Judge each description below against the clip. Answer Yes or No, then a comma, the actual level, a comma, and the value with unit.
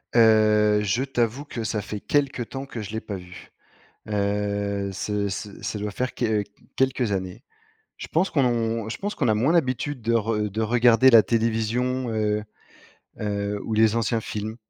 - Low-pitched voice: Yes, low, 110 Hz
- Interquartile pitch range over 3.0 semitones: No, average, 2.7 semitones